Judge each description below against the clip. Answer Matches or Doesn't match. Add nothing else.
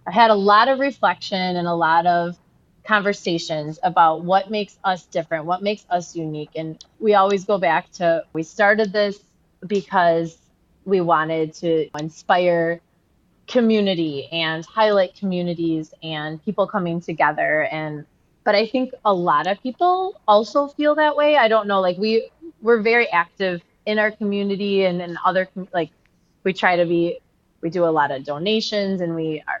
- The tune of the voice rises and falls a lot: Doesn't match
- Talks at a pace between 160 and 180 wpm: Matches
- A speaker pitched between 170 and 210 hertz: Matches